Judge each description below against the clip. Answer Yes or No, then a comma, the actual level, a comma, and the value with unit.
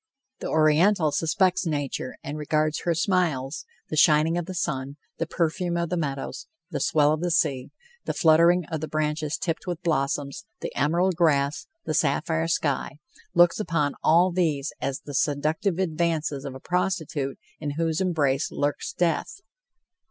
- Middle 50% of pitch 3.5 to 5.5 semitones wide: No, average, 3.0 semitones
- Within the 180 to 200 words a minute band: No, average, 160 wpm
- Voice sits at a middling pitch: Yes, medium, 155 Hz